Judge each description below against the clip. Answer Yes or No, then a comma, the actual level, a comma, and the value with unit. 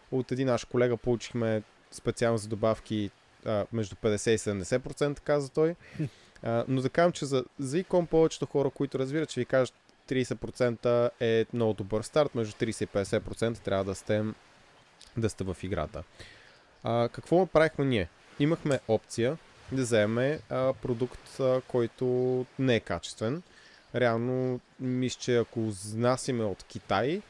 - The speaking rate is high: No, average, 145 wpm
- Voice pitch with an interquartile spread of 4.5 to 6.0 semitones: No, average, 3.2 semitones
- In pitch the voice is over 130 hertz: No, low, 120 Hz